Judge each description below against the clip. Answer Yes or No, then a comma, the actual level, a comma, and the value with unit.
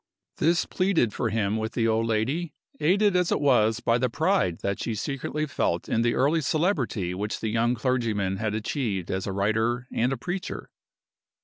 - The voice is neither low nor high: No, low, 115 Hz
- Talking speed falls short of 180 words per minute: No, average, 185 wpm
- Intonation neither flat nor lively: No, wide, 5.7 semitones